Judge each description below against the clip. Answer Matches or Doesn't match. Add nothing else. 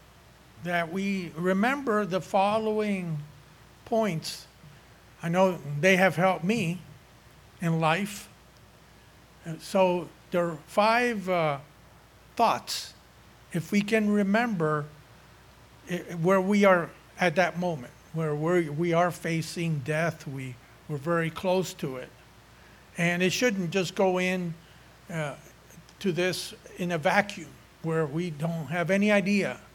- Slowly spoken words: Matches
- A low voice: Doesn't match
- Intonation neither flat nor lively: Matches